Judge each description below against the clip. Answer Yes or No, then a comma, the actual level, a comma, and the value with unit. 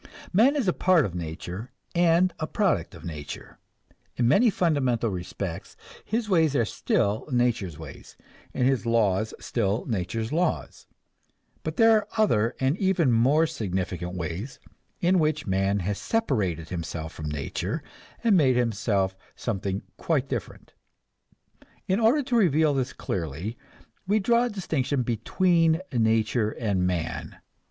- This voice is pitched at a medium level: No, low, 120 Hz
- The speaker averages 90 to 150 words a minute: Yes, average, 140 wpm